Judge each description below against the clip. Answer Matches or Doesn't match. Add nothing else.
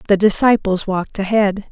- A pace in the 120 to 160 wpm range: Matches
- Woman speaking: Matches